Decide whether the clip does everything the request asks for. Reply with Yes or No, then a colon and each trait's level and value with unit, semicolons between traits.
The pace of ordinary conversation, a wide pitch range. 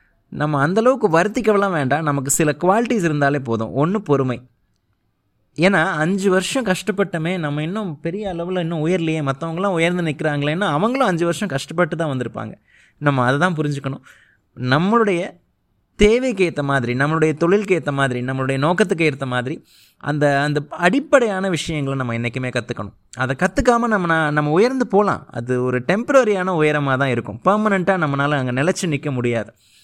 No: fast, 145 wpm; wide, 5.7 semitones